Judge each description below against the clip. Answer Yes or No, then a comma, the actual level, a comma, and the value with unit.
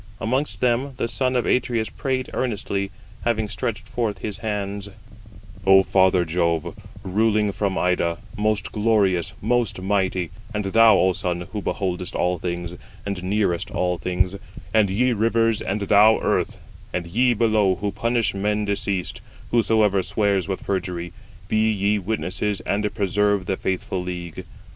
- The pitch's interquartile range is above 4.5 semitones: No, average, 3.0 semitones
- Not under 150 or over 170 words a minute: No, average, 140 wpm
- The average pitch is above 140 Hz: No, low, 100 Hz